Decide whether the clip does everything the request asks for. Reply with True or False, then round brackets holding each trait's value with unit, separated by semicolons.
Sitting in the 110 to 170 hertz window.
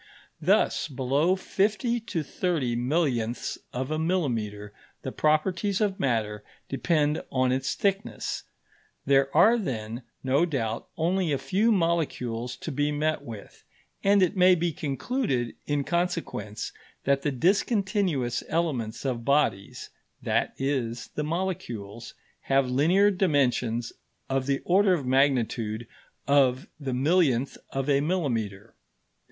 True (140 Hz)